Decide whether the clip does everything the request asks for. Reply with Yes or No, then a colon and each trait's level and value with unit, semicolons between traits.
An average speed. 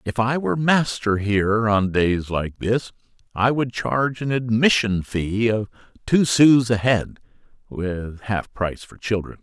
Yes: average, 160 wpm